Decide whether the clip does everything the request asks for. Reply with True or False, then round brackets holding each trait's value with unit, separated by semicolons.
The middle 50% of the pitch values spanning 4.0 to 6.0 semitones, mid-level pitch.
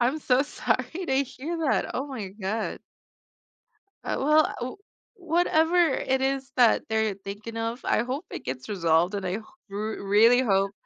False (5.1 semitones; 230 Hz)